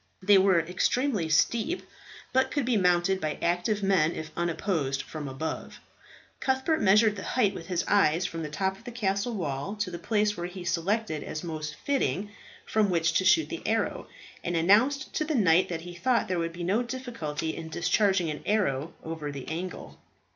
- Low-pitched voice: No, medium, 185 Hz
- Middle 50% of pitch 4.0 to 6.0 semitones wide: Yes, average, 4.6 semitones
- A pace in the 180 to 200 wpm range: Yes, average, 190 wpm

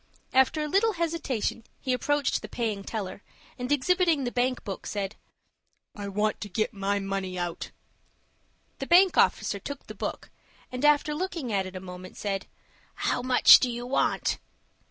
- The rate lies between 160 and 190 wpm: Yes, average, 165 wpm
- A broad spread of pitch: Yes, wide, 6.7 semitones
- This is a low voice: No, high, 245 Hz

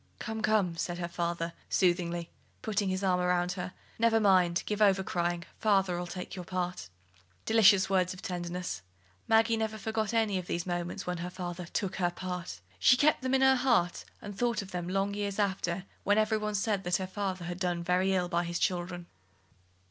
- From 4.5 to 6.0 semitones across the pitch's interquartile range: No, average, 2.8 semitones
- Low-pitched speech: No, medium, 185 Hz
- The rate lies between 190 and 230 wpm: Yes, average, 195 wpm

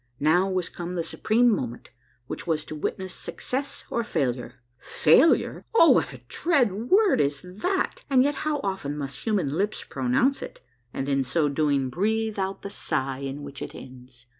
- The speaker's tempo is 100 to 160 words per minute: No, average, 175 wpm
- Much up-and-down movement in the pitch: Yes, wide, 8.3 semitones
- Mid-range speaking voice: Yes, medium, 170 Hz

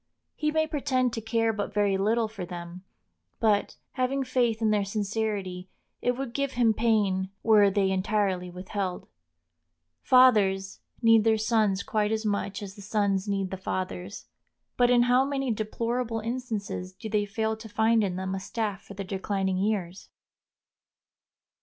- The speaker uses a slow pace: No, average, 160 wpm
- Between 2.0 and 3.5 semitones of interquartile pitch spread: Yes, average, 3.0 semitones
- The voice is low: No, high, 210 Hz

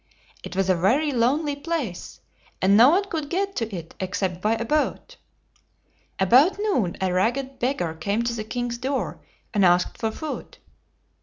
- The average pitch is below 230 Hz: No, high, 235 Hz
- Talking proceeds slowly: No, average, 165 wpm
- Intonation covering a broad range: Yes, wide, 7.3 semitones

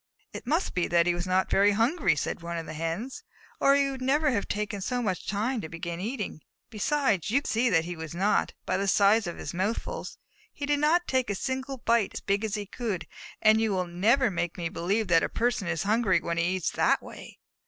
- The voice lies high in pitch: Yes, high, 205 Hz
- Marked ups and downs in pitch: Yes, wide, 5.9 semitones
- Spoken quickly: Yes, fast, 240 wpm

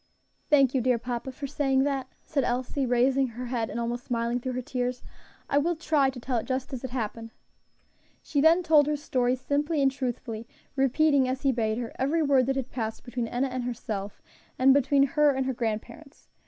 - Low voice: No, very high, 260 Hz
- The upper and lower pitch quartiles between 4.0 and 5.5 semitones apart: No, narrow, 2.4 semitones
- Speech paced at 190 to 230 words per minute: Yes, fast, 205 wpm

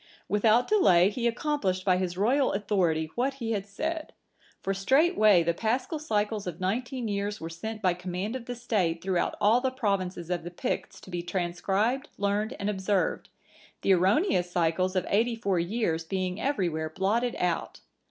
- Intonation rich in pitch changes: No, average, 4.6 semitones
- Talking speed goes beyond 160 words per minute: Yes, average, 170 wpm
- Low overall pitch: No, high, 200 Hz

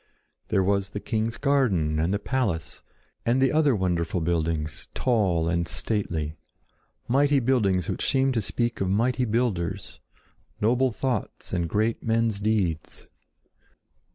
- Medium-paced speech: No, slow, 125 wpm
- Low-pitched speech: Yes, low, 105 Hz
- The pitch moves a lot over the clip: Yes, wide, 6.1 semitones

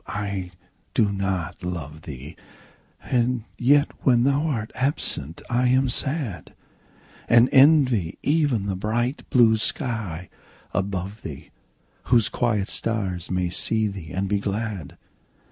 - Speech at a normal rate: No, slow, 125 wpm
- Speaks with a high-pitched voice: No, low, 110 Hz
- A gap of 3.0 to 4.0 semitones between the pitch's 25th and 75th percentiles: No, average, 5.1 semitones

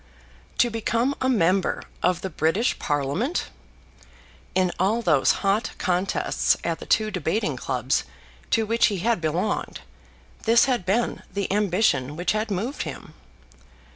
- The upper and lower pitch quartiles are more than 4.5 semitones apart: Yes, average, 5.1 semitones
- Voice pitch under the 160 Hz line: No, high, 195 Hz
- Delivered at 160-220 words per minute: No, average, 140 wpm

